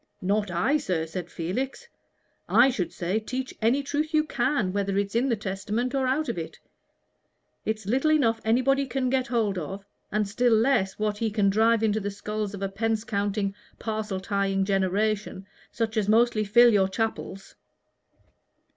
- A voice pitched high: Yes, high, 215 Hz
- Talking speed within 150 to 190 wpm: Yes, average, 170 wpm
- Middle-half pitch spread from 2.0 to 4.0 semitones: Yes, average, 3.6 semitones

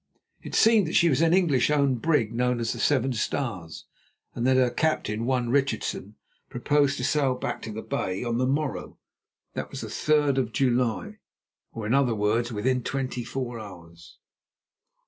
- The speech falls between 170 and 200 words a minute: Yes, average, 175 wpm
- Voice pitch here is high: No, low, 125 Hz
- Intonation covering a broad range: No, average, 3.7 semitones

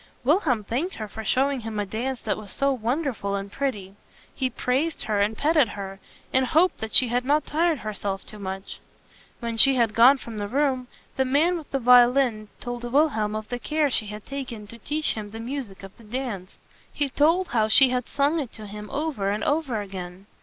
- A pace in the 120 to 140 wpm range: No, fast, 205 wpm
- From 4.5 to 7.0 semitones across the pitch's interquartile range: Yes, average, 4.8 semitones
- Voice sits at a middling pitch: No, high, 245 Hz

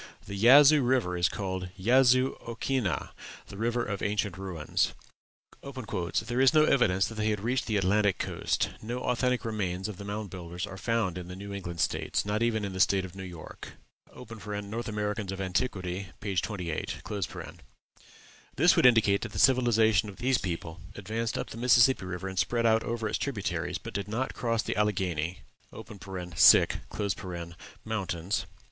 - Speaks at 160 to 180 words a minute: Yes, average, 165 wpm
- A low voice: Yes, low, 105 Hz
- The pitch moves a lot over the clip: No, average, 3.9 semitones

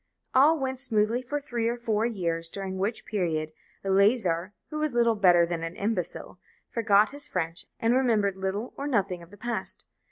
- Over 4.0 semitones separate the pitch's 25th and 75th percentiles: Yes, average, 4.7 semitones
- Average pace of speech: Yes, average, 180 wpm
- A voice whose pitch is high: Yes, high, 210 Hz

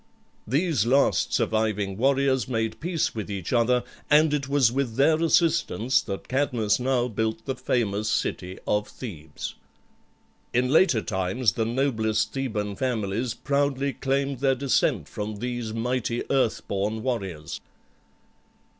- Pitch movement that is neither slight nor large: Yes, average, 4.0 semitones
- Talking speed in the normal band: No, slow, 130 wpm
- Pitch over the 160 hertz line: No, low, 120 Hz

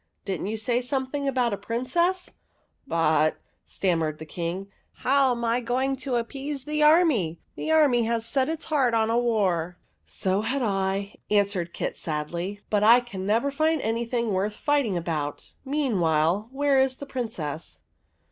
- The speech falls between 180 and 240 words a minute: Yes, average, 185 wpm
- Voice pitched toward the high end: Yes, high, 230 Hz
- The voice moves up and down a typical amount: No, wide, 6.2 semitones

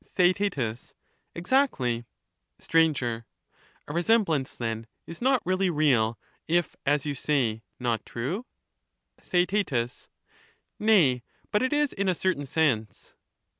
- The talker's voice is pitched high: No, medium, 155 Hz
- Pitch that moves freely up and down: Yes, wide, 7.5 semitones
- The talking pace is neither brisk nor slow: No, slow, 110 wpm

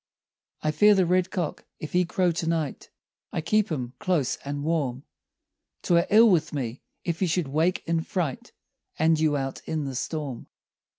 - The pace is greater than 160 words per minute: Yes, average, 170 wpm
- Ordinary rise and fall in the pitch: Yes, average, 3.7 semitones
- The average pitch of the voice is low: No, medium, 160 Hz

